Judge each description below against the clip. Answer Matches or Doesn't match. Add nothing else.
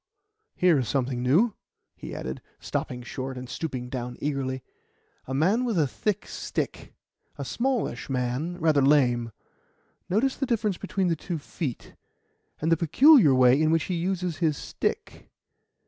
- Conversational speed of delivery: Matches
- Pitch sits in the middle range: Matches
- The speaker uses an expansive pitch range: Matches